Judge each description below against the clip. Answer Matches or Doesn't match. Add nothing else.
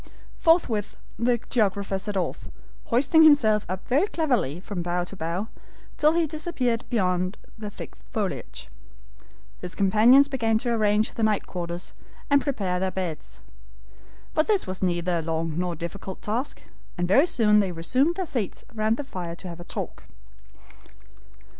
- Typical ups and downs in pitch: Doesn't match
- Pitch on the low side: Doesn't match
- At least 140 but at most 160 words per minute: Matches